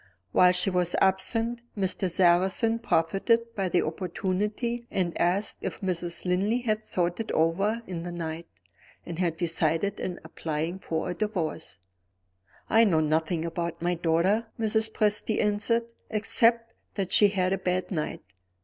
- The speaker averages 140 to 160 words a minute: Yes, average, 150 wpm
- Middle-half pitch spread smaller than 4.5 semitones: Yes, average, 3.9 semitones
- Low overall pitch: No, medium, 185 Hz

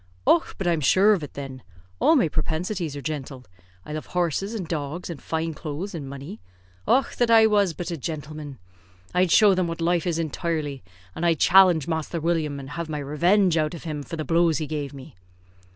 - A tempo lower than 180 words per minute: No, fast, 205 wpm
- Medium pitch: Yes, medium, 165 Hz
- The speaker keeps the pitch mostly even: No, average, 3.0 semitones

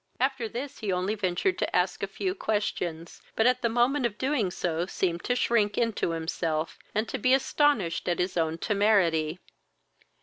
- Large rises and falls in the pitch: Yes, wide, 6.0 semitones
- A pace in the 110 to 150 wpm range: No, average, 175 wpm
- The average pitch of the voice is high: Yes, high, 205 Hz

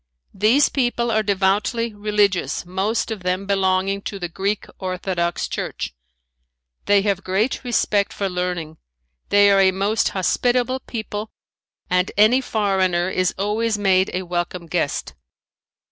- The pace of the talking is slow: Yes, slow, 130 wpm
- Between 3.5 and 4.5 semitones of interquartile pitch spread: No, narrow, 2.6 semitones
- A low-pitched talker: No, high, 195 Hz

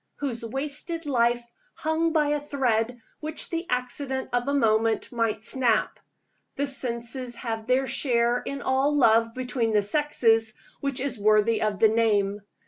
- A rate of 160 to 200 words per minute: No, average, 150 wpm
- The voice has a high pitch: Yes, high, 245 Hz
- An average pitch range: Yes, average, 3.8 semitones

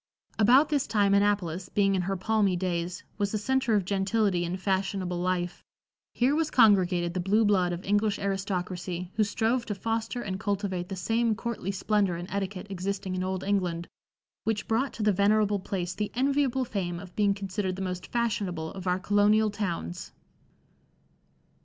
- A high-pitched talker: Yes, high, 200 Hz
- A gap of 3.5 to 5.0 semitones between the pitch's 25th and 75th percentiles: No, average, 2.7 semitones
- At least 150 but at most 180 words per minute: Yes, average, 170 wpm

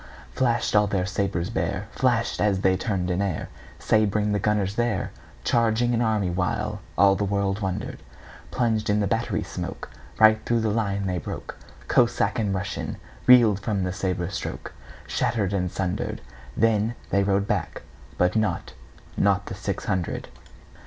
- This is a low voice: Yes, low, 100 Hz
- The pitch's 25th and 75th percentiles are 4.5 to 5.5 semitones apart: No, average, 2.8 semitones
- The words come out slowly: Yes, slow, 125 wpm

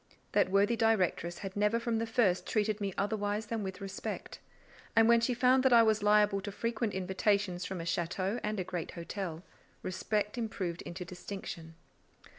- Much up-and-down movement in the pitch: No, average, 3.1 semitones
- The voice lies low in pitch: No, high, 205 Hz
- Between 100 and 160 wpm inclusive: No, average, 175 wpm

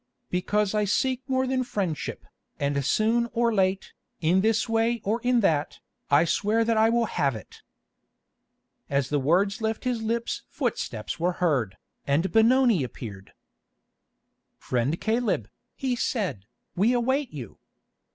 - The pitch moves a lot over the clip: Yes, wide, 7.4 semitones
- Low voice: No, high, 210 Hz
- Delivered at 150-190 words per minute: No, average, 140 wpm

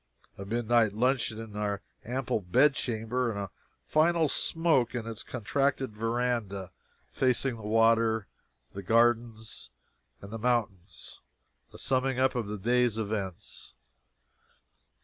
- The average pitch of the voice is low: Yes, low, 115 Hz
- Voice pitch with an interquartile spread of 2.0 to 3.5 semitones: Yes, average, 2.9 semitones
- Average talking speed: No, slow, 120 wpm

